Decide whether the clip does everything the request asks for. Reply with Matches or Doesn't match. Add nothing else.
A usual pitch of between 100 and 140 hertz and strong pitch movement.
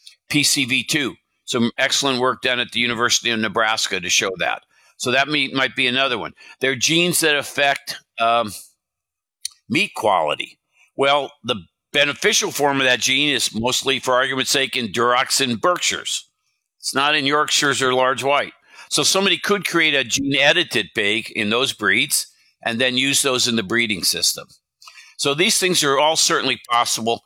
Doesn't match